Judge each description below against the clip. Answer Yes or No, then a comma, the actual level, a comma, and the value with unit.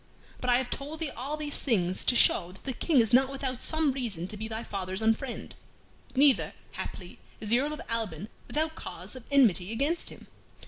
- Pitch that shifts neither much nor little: Yes, average, 4.3 semitones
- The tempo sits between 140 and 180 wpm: No, average, 200 wpm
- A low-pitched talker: No, very high, 250 Hz